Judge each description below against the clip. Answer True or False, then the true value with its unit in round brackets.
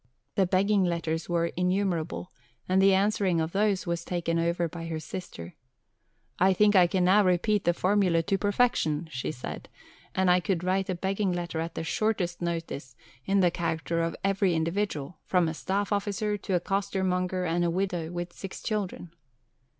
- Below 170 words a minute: False (175 wpm)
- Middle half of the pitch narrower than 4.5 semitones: True (2.6 semitones)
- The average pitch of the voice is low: False (180 Hz)